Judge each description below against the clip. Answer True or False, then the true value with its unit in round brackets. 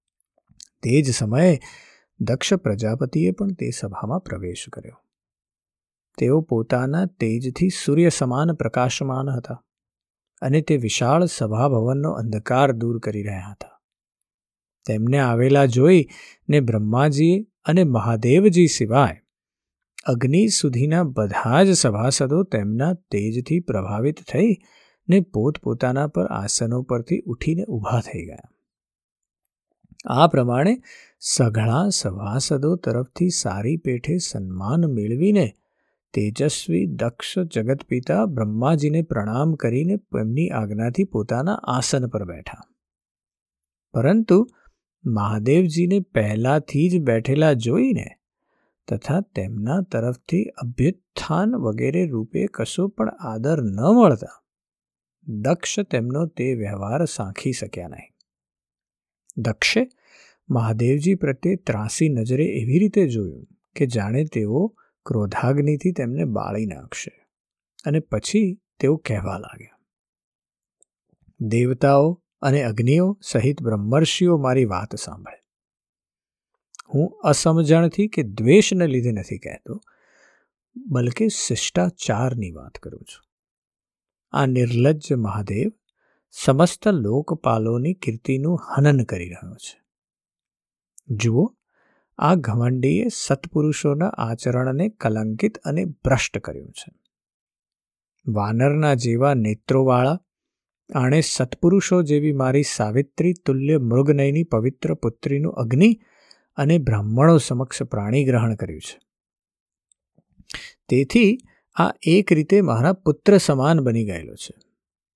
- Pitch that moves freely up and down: True (6.8 semitones)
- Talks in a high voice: False (135 Hz)